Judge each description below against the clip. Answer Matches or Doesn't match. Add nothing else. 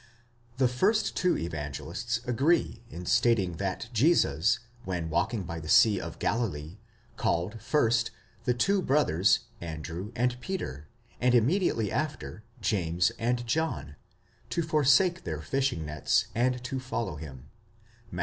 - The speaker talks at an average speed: Doesn't match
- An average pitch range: Doesn't match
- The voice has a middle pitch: Doesn't match